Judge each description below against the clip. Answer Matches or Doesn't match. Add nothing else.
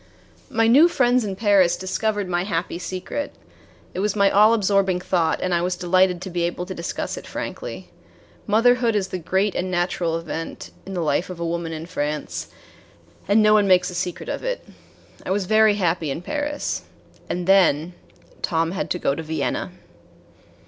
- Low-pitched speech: Doesn't match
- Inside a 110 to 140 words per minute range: Doesn't match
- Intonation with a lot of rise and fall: Doesn't match